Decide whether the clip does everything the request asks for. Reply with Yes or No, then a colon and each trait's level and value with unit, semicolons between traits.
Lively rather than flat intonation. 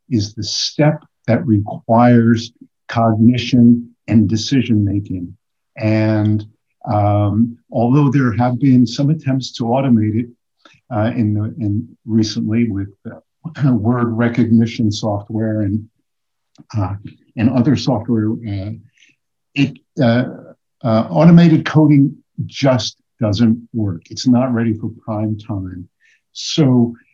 No: narrow, 2.6 semitones